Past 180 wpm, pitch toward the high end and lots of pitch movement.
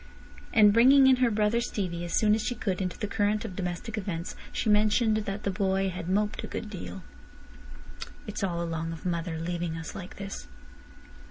No: average, 190 wpm; high, 195 Hz; average, 3.5 semitones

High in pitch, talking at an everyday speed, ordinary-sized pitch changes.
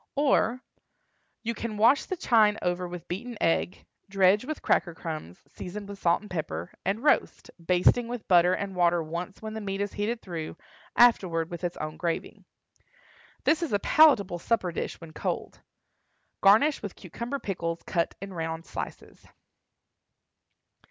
Yes: high, 195 Hz; average, 155 wpm; average, 4.7 semitones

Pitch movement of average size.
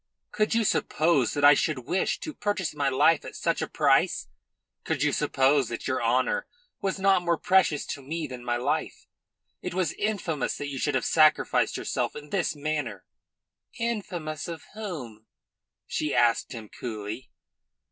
No: wide, 6.0 semitones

